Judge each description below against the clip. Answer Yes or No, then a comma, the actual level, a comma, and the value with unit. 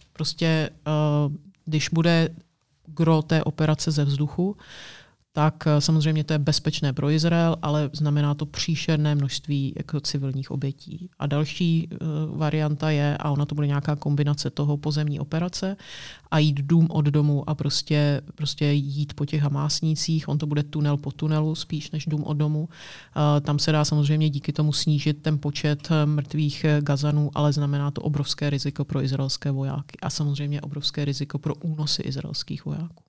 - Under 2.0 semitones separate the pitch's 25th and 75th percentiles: Yes, narrow, 1.3 semitones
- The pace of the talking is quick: No, average, 160 wpm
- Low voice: No, medium, 150 Hz